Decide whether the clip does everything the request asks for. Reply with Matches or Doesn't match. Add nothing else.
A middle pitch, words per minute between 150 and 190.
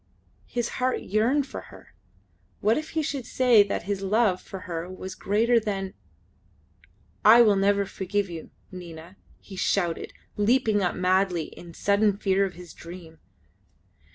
Doesn't match